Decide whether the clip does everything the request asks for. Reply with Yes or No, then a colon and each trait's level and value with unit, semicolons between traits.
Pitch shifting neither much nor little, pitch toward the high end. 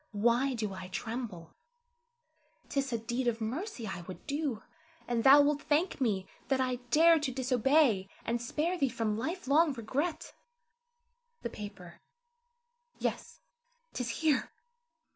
Yes: average, 4.7 semitones; very high, 250 Hz